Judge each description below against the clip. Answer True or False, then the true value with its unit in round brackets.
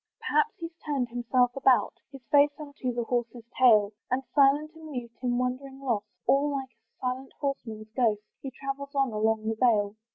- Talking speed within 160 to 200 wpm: True (180 wpm)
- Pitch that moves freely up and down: False (2.9 semitones)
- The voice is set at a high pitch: True (255 Hz)